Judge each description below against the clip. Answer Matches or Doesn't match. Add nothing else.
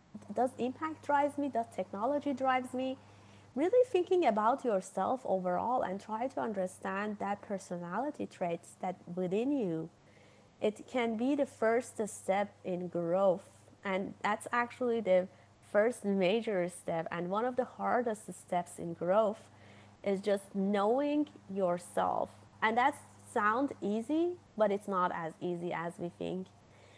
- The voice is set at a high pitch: Matches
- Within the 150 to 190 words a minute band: Doesn't match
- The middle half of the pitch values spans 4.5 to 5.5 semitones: Matches